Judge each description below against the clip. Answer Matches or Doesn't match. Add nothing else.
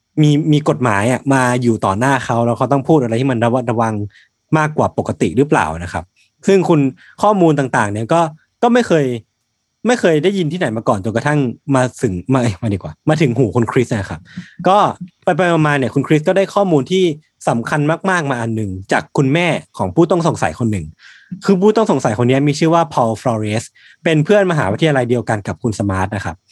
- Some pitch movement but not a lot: Doesn't match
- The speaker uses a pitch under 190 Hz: Matches